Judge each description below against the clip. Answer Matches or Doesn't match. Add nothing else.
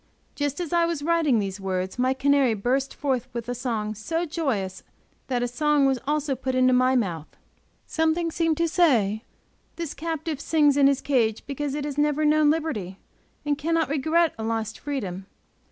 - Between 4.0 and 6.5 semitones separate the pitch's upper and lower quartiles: Matches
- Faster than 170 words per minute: Matches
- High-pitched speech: Matches